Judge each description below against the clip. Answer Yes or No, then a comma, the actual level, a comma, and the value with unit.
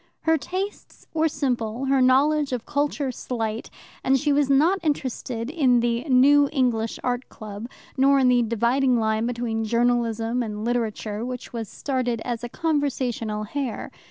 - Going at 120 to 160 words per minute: Yes, average, 155 wpm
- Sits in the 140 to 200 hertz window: No, very high, 250 Hz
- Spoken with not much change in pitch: No, average, 3.3 semitones